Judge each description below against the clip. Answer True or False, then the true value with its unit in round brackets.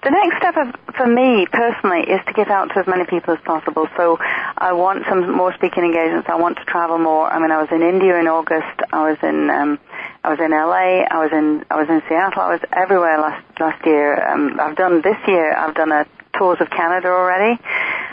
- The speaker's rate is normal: False (230 wpm)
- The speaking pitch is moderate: True (170 Hz)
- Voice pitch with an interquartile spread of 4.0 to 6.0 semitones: False (3.2 semitones)